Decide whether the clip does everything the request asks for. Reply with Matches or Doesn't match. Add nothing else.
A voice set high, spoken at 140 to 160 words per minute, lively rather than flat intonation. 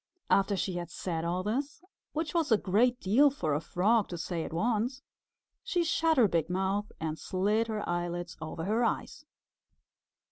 Doesn't match